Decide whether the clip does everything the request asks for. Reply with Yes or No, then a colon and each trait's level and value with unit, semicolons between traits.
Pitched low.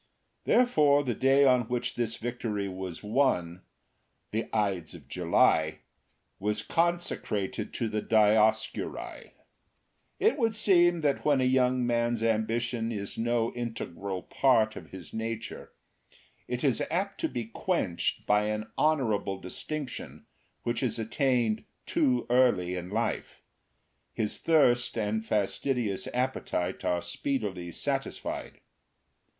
Yes: low, 115 Hz